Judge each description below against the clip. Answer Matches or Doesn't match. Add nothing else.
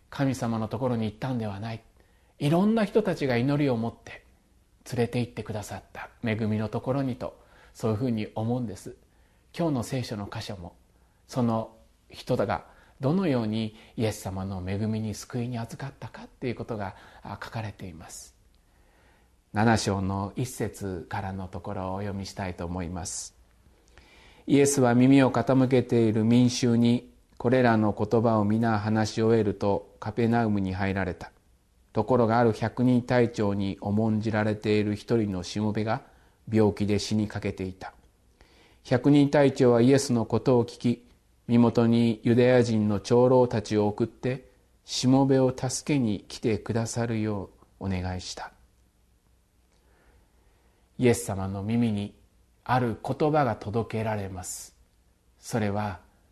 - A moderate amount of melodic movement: Matches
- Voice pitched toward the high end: Doesn't match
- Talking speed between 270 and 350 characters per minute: Matches